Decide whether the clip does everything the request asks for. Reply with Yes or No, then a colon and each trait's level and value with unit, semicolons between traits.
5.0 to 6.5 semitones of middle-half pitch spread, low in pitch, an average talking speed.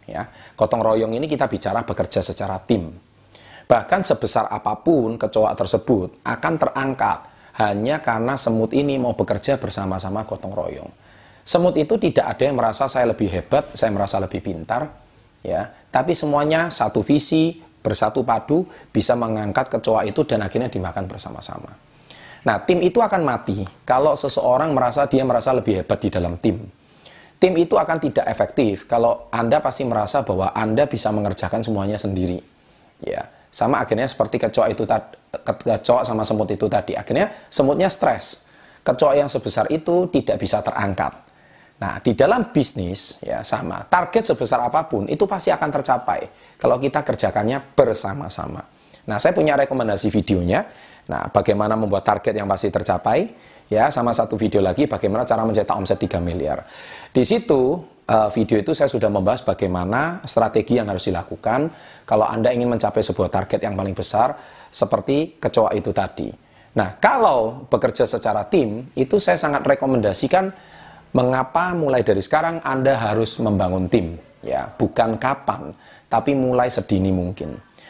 No: average, 5.3 semitones; low, 115 Hz; fast, 150 wpm